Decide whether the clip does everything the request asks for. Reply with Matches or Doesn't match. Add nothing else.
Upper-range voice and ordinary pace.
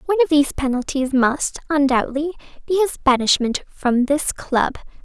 Matches